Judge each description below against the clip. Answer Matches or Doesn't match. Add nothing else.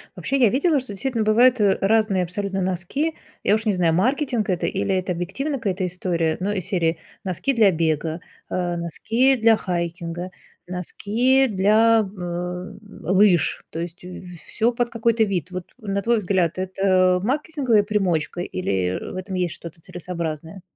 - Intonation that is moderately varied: Matches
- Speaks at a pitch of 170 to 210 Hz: Matches